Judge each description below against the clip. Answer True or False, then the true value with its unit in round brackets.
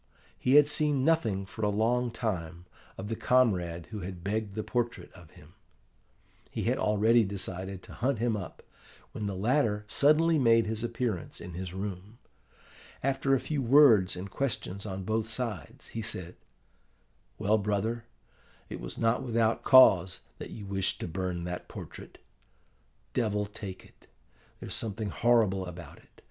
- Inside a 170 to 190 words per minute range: False (155 wpm)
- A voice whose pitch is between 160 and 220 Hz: False (105 Hz)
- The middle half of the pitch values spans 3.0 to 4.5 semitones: True (4.0 semitones)